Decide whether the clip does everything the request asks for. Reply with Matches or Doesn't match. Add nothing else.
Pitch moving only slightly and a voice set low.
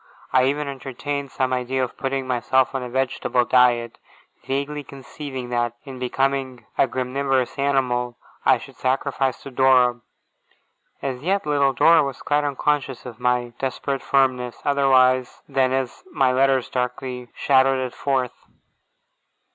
Matches